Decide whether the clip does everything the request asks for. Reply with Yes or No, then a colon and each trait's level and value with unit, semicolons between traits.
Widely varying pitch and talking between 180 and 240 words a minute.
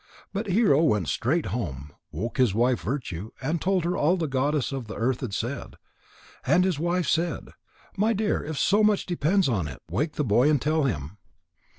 Yes: wide, 7.3 semitones; average, 200 wpm